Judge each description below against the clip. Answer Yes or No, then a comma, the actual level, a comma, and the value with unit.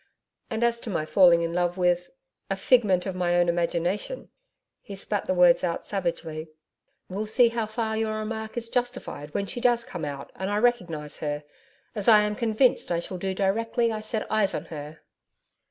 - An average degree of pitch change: Yes, average, 4.3 semitones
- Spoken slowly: No, average, 190 wpm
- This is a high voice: Yes, high, 195 Hz